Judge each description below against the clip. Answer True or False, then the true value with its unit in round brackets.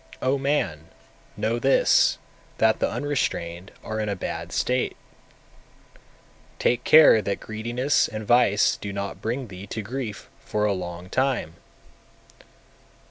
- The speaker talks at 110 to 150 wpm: True (135 wpm)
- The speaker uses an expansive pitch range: False (4.1 semitones)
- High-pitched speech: False (110 Hz)